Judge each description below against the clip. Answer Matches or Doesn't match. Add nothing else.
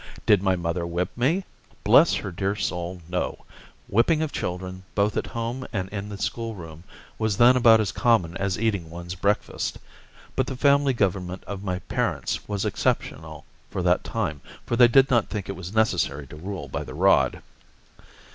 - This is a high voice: Doesn't match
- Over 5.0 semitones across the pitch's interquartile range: Doesn't match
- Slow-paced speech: Doesn't match